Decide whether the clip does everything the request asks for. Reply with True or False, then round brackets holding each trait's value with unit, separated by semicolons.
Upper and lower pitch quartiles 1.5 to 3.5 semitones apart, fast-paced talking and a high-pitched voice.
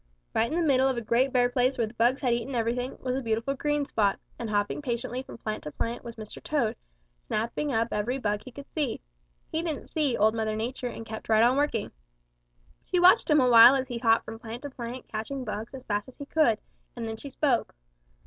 True (3.2 semitones; 235 wpm; 240 Hz)